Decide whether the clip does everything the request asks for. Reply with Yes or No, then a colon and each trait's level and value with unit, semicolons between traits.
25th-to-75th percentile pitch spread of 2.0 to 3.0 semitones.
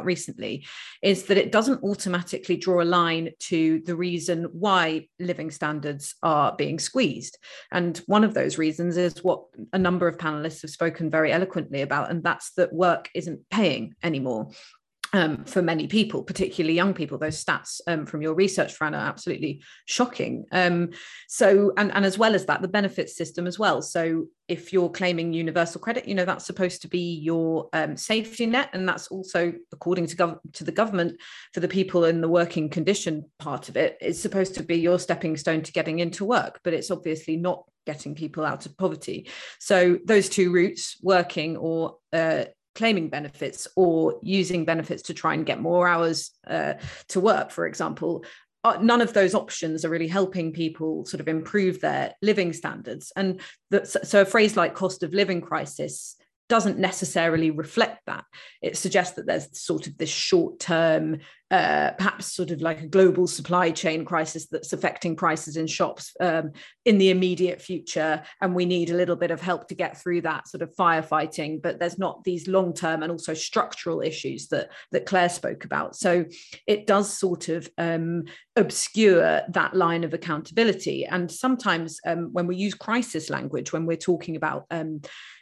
Yes: average, 2.7 semitones